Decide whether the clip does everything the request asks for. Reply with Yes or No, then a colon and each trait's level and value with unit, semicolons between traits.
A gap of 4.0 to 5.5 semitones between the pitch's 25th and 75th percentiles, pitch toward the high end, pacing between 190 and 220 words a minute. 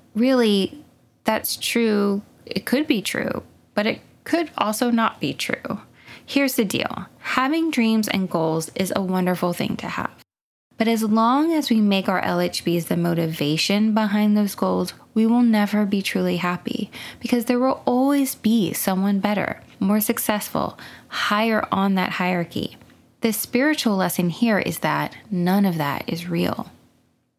No: average, 4.3 semitones; high, 210 Hz; average, 155 wpm